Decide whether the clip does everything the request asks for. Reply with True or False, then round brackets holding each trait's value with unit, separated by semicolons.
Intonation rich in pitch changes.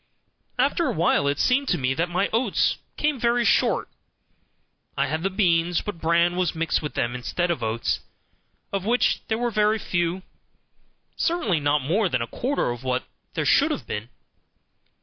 True (7.1 semitones)